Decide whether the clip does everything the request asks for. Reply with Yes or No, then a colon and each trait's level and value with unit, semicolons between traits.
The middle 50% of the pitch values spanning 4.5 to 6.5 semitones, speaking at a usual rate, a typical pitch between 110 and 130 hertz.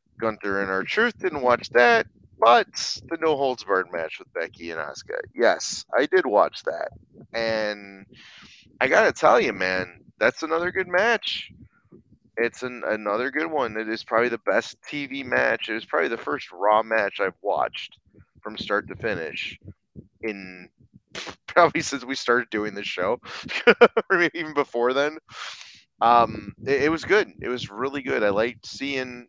Yes: wide, 5.4 semitones; average, 165 wpm; low, 120 Hz